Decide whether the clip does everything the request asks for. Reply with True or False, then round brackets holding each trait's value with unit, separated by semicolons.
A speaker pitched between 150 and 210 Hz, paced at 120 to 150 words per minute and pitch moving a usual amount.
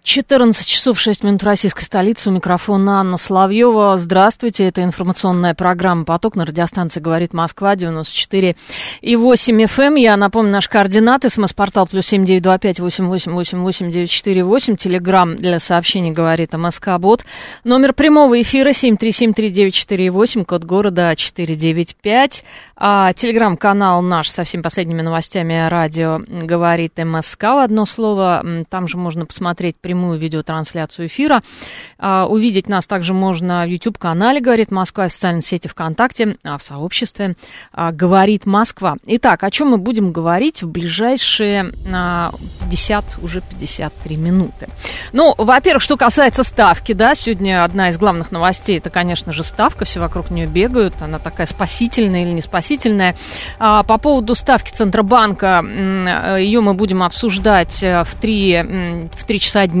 True (190 Hz; 130 wpm; 4.0 semitones)